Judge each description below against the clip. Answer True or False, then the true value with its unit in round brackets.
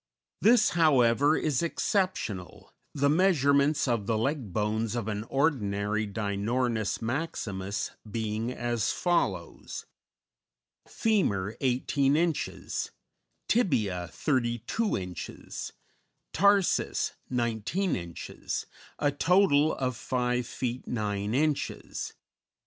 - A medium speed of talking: False (90 wpm)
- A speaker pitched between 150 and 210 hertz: False (125 Hz)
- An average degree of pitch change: False (6.1 semitones)